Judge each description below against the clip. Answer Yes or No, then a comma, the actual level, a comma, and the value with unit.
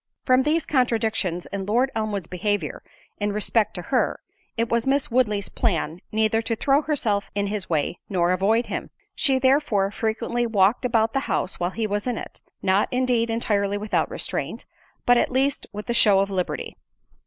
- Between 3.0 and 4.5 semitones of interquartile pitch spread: Yes, average, 3.5 semitones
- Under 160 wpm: No, average, 175 wpm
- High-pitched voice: Yes, high, 220 Hz